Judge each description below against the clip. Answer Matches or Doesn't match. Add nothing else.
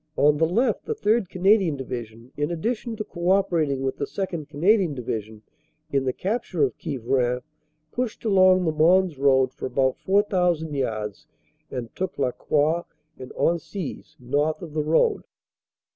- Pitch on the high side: Doesn't match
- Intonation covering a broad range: Matches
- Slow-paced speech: Doesn't match